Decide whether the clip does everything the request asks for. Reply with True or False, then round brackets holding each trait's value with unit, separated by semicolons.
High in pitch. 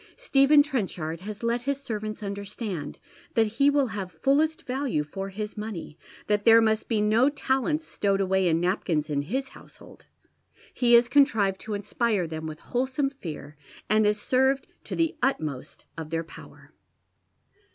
True (215 Hz)